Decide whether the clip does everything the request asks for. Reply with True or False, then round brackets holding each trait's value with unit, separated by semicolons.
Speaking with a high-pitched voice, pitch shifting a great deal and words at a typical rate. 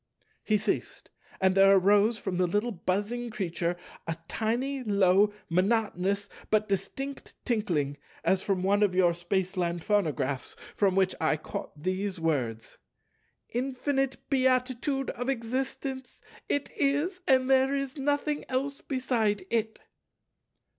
False (210 Hz; 5.9 semitones; 125 wpm)